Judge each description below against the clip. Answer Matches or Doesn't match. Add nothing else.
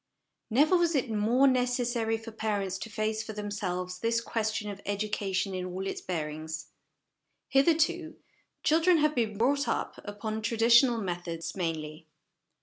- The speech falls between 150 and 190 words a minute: Doesn't match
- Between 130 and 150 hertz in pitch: Doesn't match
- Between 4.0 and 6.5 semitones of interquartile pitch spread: Matches